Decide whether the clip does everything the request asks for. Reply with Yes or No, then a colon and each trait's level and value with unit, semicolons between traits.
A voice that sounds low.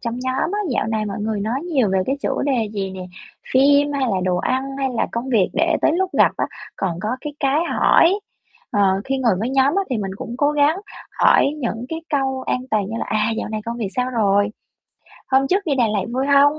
No: very high, 250 Hz